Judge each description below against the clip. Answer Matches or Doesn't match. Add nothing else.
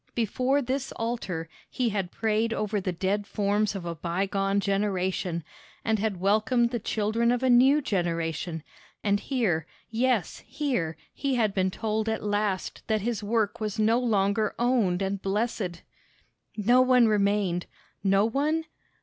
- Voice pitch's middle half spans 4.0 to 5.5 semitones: Doesn't match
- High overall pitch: Matches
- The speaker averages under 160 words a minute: Matches